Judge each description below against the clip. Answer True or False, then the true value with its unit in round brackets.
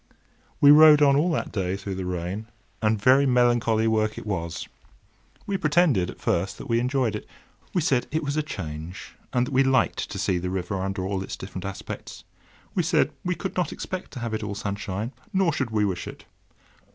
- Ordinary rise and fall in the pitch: False (6.6 semitones)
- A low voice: True (110 Hz)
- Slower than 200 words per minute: False (205 wpm)